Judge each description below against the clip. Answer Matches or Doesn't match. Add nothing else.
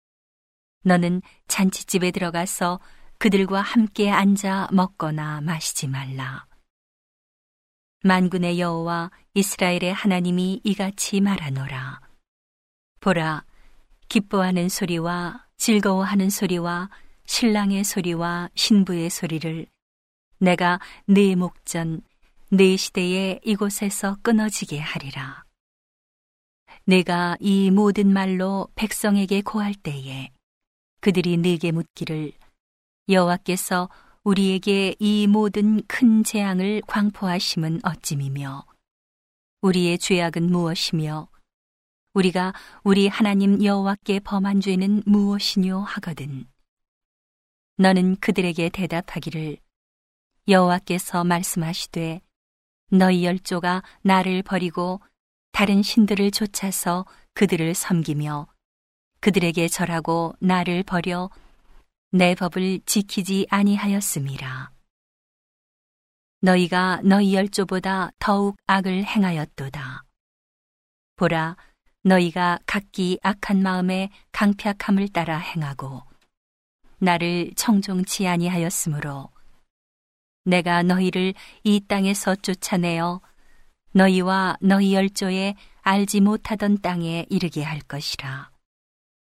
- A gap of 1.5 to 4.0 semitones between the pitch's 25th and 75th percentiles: Matches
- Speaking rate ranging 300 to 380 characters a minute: Doesn't match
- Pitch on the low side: Doesn't match